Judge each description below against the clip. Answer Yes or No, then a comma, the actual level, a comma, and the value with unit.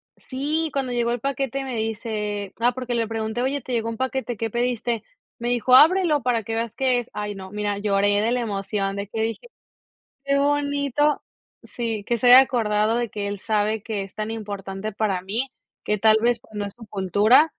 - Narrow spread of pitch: No, average, 3.4 semitones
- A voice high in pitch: Yes, high, 225 Hz